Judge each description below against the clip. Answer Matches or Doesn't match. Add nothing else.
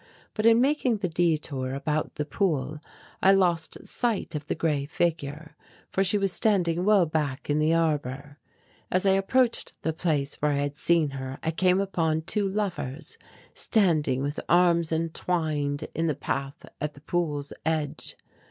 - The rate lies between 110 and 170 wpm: Matches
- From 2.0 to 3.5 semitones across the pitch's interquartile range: Doesn't match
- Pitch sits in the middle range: Matches